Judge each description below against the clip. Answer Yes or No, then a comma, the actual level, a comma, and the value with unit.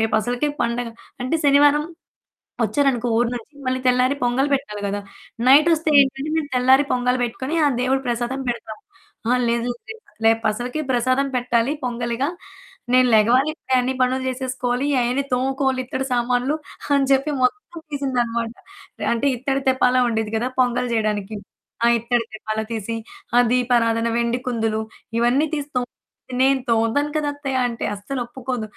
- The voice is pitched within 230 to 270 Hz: Yes, very high, 250 Hz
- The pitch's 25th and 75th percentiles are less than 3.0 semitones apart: Yes, narrow, 2.4 semitones